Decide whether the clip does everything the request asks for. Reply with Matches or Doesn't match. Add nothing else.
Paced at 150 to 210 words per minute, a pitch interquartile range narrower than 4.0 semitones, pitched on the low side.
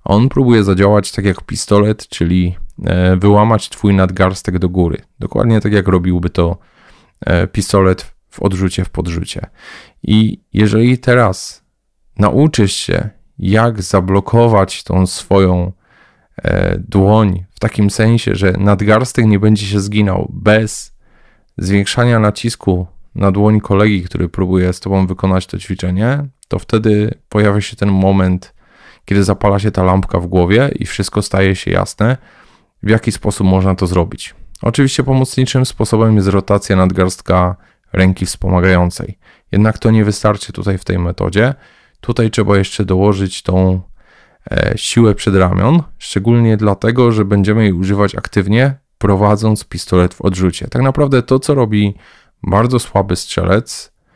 Doesn't match